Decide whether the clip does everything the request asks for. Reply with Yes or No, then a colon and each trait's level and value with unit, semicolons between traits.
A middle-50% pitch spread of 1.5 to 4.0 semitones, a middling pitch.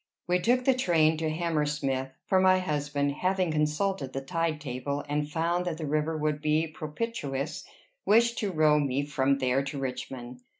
Yes: average, 3.6 semitones; medium, 150 Hz